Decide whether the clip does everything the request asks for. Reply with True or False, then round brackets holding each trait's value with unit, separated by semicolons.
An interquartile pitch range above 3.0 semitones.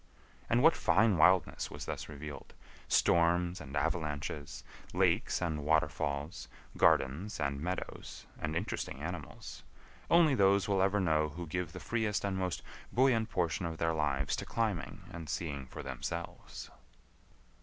True (4.2 semitones)